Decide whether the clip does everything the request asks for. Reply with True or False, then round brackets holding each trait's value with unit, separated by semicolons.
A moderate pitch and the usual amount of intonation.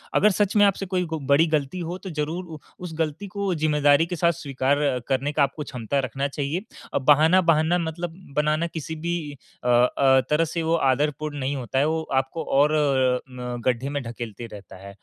True (150 Hz; 3.7 semitones)